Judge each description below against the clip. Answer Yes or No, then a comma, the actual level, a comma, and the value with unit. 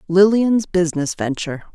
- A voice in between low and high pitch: Yes, medium, 180 Hz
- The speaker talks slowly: Yes, slow, 105 wpm